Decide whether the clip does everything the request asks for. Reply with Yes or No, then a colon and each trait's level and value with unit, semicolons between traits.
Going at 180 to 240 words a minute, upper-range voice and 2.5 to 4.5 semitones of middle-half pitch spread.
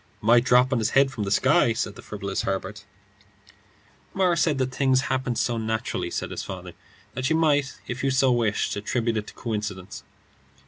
No: average, 185 wpm; low, 120 Hz; average, 3.7 semitones